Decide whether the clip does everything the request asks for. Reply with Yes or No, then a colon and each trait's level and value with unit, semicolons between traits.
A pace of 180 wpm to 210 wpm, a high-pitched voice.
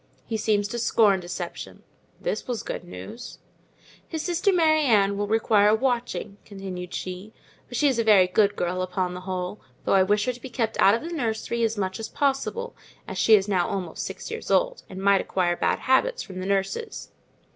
Yes: average, 200 wpm; high, 210 Hz